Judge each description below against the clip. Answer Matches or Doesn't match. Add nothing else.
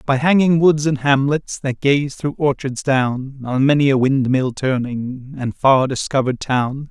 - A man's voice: Matches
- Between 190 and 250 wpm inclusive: Doesn't match